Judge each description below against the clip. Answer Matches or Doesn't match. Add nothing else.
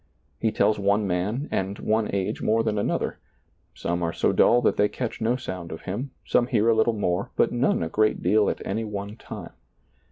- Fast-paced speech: Matches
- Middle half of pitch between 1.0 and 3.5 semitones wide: Matches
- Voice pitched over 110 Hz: Doesn't match